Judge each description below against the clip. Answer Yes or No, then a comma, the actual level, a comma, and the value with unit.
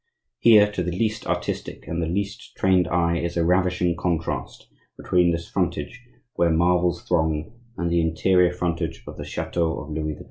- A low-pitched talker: Yes, very low, 85 Hz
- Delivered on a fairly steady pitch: Yes, narrow, 1.6 semitones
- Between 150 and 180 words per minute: Yes, average, 175 wpm